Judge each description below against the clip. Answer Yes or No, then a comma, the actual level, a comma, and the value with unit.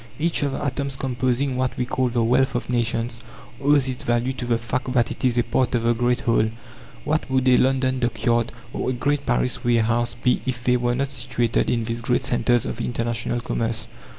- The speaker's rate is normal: No, fast, 210 wpm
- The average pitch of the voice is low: Yes, low, 125 Hz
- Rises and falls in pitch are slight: Yes, narrow, 1.7 semitones